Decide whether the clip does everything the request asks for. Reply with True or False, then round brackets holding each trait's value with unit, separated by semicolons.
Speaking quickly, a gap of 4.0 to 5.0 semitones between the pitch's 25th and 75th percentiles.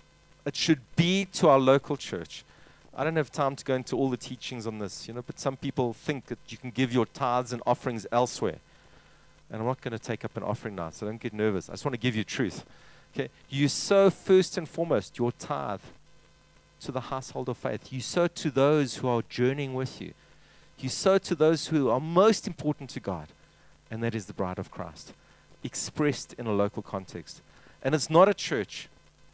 True (215 wpm; 4.7 semitones)